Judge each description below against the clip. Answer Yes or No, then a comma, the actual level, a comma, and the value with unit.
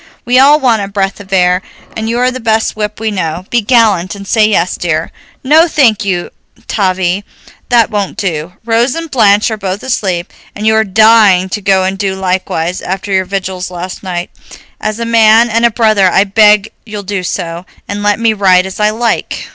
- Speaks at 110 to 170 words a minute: No, fast, 205 wpm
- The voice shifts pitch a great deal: No, average, 3.1 semitones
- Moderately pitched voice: No, high, 205 Hz